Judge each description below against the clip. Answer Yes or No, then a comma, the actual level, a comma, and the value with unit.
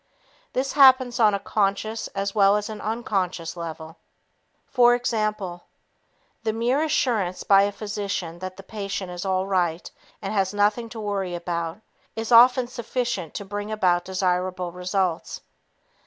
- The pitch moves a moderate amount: Yes, average, 3.5 semitones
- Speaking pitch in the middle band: No, high, 200 Hz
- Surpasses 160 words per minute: No, average, 140 wpm